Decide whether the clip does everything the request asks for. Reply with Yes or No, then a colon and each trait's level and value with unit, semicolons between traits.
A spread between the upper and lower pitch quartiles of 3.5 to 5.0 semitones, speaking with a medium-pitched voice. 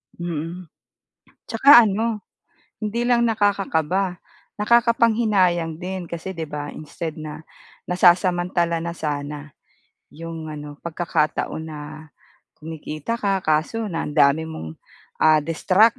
Yes: average, 4.6 semitones; medium, 170 Hz